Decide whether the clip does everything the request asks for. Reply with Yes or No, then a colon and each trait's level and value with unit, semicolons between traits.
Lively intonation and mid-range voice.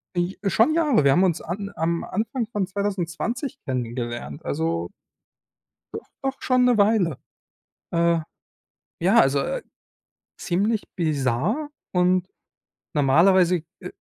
Yes: wide, 6.0 semitones; medium, 180 Hz